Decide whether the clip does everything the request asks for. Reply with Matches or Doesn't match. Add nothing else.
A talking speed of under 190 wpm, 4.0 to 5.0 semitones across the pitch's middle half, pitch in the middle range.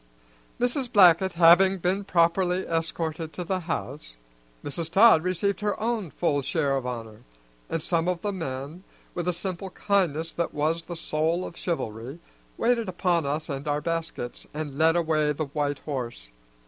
Doesn't match